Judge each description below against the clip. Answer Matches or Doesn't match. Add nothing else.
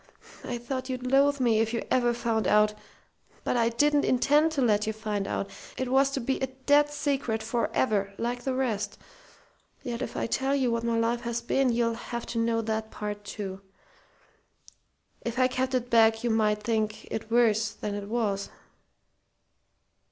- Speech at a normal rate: Matches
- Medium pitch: Doesn't match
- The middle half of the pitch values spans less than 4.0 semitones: Matches